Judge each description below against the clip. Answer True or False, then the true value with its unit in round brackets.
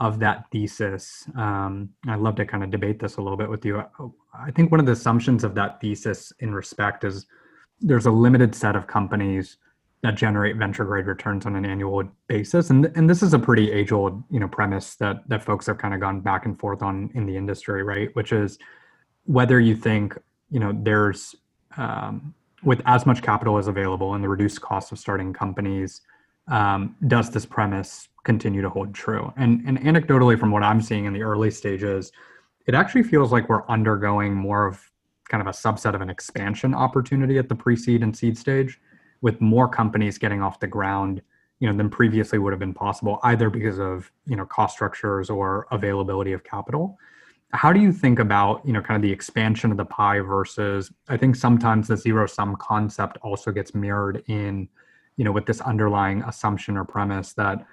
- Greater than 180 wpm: True (200 wpm)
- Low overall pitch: True (105 Hz)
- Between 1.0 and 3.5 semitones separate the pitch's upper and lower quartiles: True (2.7 semitones)